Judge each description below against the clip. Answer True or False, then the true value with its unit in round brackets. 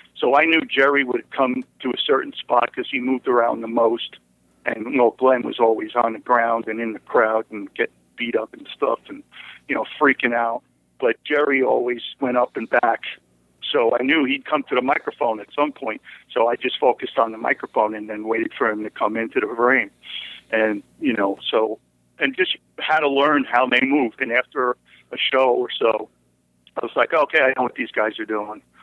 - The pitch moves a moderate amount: True (4.0 semitones)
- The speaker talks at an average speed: False (215 wpm)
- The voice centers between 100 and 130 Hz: True (115 Hz)